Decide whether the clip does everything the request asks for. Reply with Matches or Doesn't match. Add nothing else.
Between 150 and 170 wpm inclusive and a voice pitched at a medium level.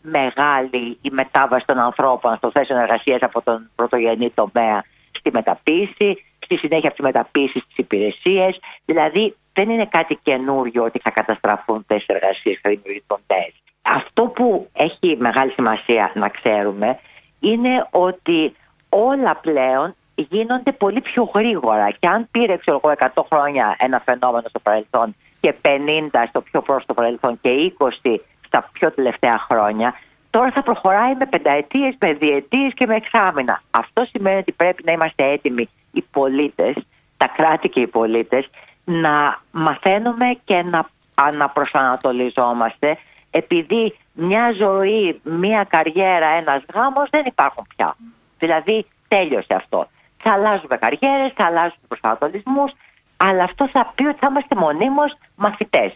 Doesn't match